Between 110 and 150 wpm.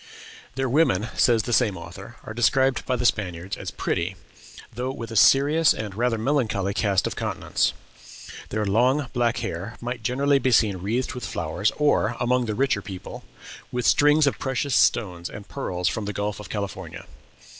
No: average, 175 wpm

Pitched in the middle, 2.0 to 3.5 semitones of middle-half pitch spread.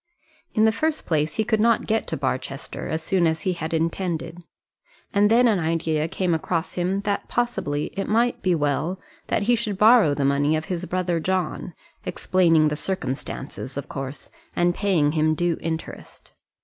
No: medium, 175 Hz; average, 4.2 semitones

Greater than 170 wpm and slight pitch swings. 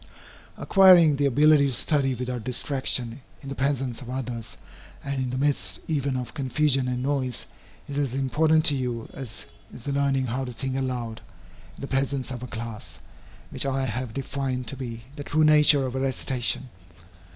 Yes: average, 180 wpm; narrow, 2.0 semitones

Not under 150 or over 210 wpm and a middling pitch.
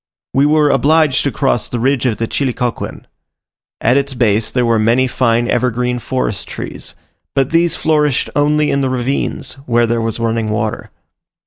No: average, 165 wpm; low, 125 Hz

